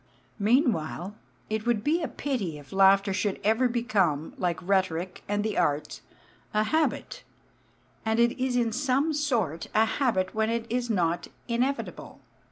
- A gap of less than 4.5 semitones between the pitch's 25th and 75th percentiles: No, average, 4.8 semitones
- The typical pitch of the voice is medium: No, high, 220 Hz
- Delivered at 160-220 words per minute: No, average, 150 wpm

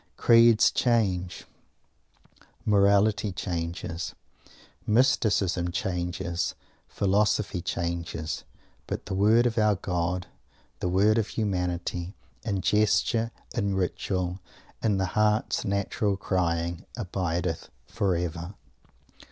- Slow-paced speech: Yes, slow, 90 wpm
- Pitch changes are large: No, average, 3.2 semitones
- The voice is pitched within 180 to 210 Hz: No, very low, 95 Hz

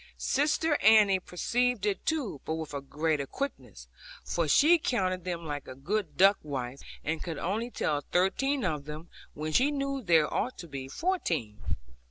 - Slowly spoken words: No, average, 170 wpm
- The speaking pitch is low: No, medium, 180 Hz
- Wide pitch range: Yes, wide, 8.6 semitones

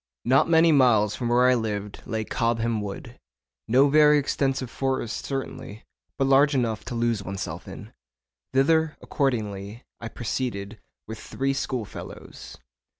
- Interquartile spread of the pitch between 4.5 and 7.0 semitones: No, average, 3.8 semitones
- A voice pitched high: No, low, 120 Hz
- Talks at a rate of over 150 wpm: No, slow, 135 wpm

